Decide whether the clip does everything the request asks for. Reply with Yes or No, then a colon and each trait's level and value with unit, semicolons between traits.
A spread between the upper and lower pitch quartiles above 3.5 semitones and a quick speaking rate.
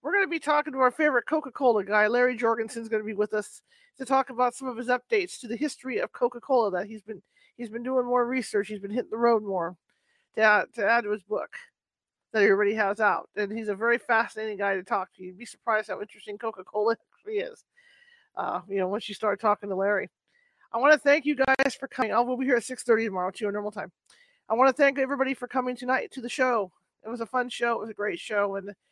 Yes: average, 4.0 semitones; fast, 255 wpm